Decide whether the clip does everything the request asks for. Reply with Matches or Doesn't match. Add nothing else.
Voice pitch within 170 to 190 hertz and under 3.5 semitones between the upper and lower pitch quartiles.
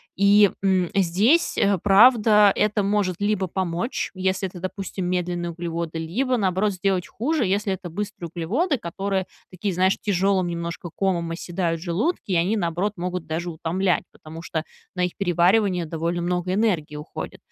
Matches